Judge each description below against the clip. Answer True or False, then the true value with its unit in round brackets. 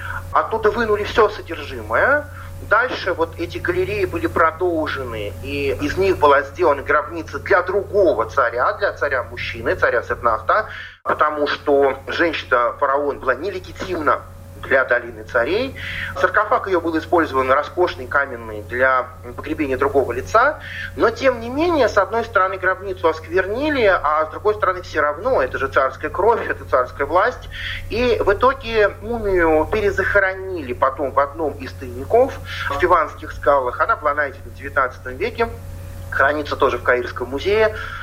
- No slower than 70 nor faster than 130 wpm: False (140 wpm)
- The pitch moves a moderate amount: False (8.8 semitones)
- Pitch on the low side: False (185 Hz)